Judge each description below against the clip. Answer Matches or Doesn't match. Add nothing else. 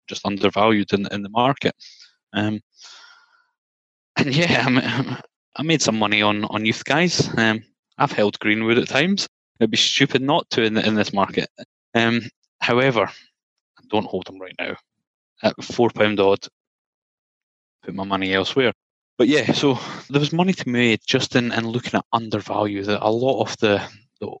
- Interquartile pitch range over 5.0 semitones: Doesn't match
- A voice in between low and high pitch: Doesn't match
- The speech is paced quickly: Doesn't match